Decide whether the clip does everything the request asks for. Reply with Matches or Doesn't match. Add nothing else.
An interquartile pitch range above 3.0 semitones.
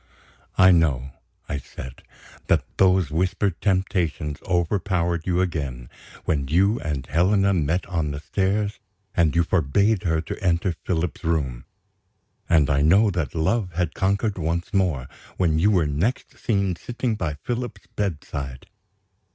Matches